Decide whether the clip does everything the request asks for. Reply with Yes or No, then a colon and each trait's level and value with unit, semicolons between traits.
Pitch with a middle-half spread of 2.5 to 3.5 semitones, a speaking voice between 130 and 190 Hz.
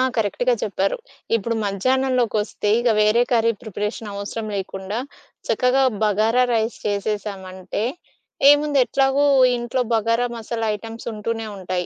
No: average, 2.9 semitones; high, 225 Hz